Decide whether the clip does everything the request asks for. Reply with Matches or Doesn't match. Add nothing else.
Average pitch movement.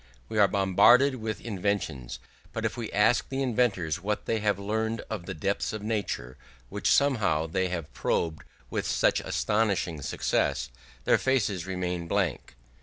Matches